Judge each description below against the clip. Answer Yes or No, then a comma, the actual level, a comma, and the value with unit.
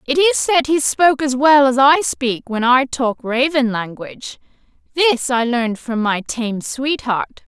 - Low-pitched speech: No, very high, 260 Hz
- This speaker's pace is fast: No, average, 175 wpm